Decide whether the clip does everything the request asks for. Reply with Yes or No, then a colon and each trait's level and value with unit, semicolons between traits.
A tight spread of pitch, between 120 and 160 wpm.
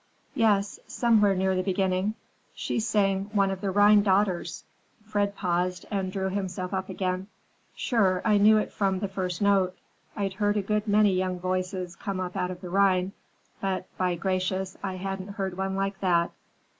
No: narrow, 1.6 semitones; average, 175 wpm